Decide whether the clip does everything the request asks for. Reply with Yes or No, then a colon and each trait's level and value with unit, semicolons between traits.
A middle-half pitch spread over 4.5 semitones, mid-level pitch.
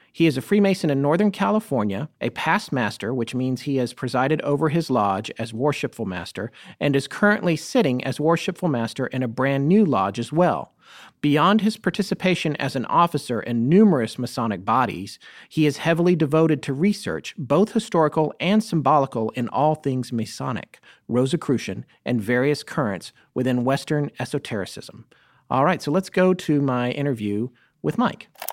Yes: average, 5.3 semitones; medium, 145 Hz